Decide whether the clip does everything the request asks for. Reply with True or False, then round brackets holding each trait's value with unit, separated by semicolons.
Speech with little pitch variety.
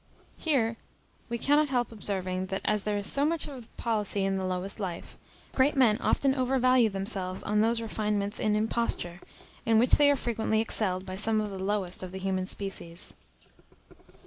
False (3.7 semitones)